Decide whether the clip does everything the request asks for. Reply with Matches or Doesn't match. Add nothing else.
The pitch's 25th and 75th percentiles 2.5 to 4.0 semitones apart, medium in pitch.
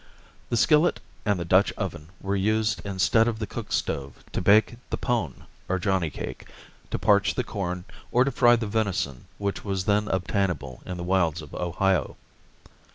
Doesn't match